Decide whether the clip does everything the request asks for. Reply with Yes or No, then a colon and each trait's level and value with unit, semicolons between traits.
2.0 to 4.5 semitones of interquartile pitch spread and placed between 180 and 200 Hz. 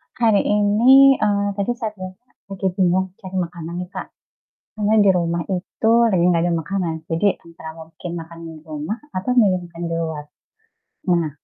Yes: average, 3.5 semitones; medium, 185 Hz